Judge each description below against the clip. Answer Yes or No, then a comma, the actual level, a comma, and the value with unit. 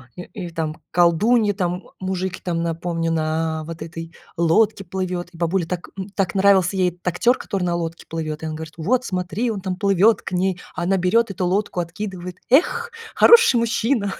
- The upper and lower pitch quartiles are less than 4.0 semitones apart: Yes, average, 3.0 semitones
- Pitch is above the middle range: No, medium, 180 Hz